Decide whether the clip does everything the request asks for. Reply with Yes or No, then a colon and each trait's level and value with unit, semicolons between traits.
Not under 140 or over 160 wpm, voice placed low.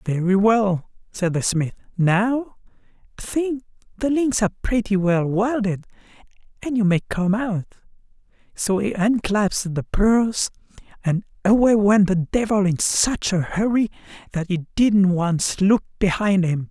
No: average, 145 wpm; high, 205 Hz